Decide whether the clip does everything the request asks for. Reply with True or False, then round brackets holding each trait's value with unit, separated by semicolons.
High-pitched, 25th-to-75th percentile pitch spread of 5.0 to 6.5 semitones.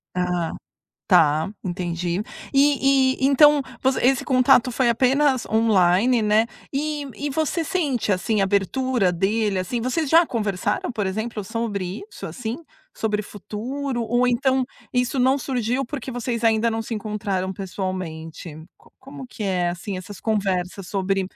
True (225 Hz; 5.4 semitones)